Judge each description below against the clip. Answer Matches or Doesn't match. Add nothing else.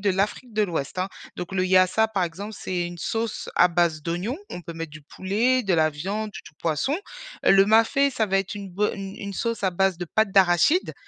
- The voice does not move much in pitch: Doesn't match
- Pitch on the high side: Matches